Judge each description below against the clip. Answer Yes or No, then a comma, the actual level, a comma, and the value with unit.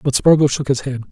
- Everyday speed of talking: No, fast, 270 wpm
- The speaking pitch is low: Yes, low, 130 Hz